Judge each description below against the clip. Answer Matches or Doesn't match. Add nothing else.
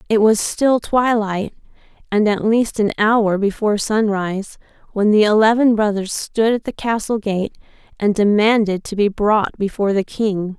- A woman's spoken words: Matches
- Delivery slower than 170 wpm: Matches